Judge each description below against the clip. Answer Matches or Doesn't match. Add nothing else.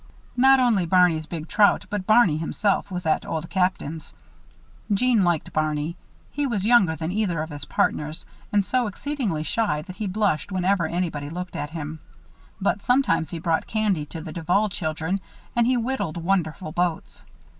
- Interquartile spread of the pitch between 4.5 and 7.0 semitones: Matches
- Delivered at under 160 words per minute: Doesn't match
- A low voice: Doesn't match